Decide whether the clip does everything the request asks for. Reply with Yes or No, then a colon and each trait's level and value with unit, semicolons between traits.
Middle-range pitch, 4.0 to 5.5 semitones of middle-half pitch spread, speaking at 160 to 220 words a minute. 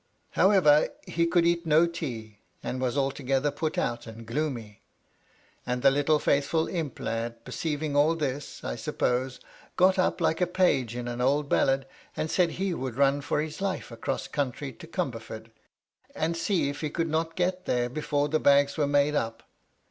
Yes: medium, 145 Hz; average, 4.4 semitones; average, 180 wpm